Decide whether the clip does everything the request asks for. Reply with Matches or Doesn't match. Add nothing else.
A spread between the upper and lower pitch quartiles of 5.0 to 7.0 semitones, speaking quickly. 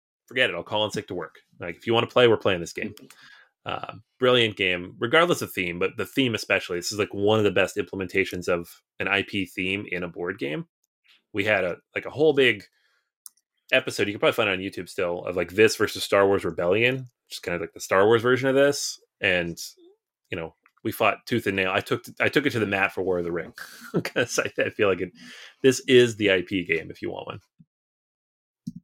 Matches